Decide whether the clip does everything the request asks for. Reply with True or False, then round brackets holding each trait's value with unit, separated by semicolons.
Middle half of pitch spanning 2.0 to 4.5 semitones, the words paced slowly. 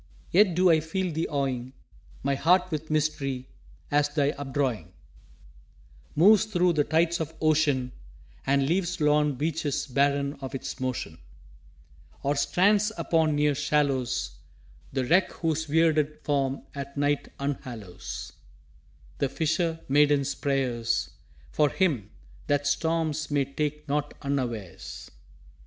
True (2.8 semitones; 120 wpm)